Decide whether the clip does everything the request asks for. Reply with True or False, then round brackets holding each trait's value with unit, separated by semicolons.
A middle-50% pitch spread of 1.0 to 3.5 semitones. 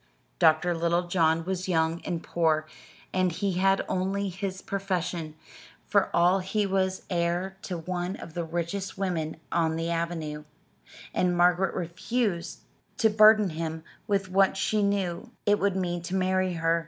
True (2.4 semitones)